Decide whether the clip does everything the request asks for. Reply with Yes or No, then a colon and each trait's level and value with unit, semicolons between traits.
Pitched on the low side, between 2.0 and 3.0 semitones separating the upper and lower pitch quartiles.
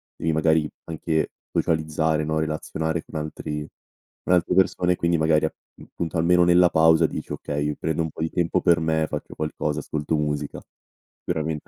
No: very low, 80 Hz; narrow, 1.4 semitones